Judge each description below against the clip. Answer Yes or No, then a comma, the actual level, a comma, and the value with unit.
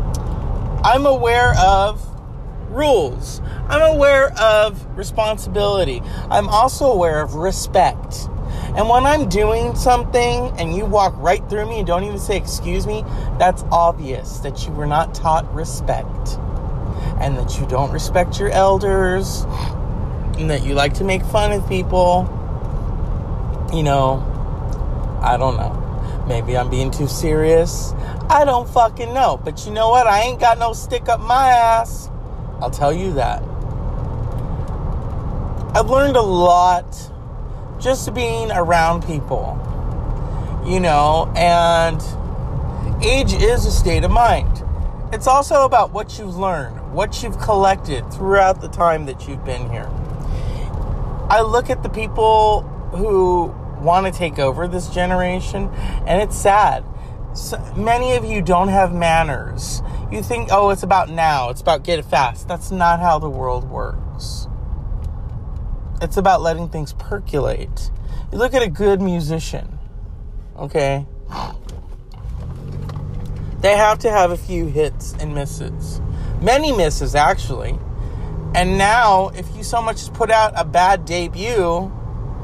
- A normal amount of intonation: No, wide, 7.3 semitones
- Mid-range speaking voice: Yes, medium, 175 Hz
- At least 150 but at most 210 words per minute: No, average, 140 wpm